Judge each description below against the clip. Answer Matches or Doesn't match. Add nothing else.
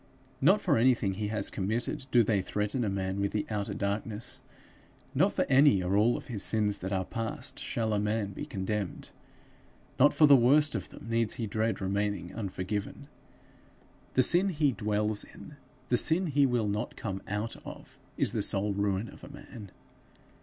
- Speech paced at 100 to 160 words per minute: Doesn't match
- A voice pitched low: Matches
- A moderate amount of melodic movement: Matches